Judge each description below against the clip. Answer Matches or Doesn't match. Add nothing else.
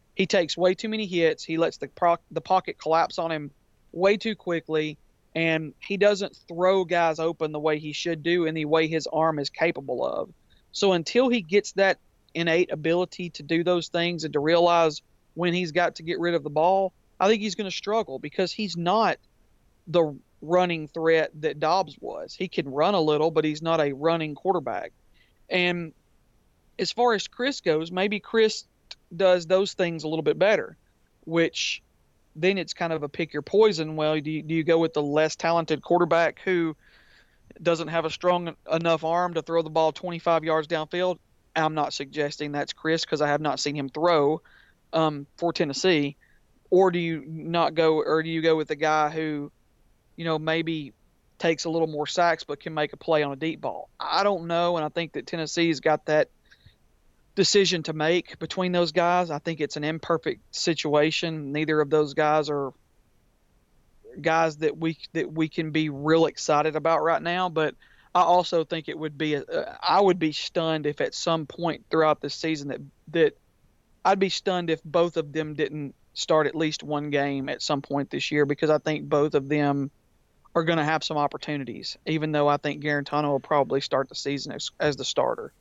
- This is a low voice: Doesn't match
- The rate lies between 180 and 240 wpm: Matches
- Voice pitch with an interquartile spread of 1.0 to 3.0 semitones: Matches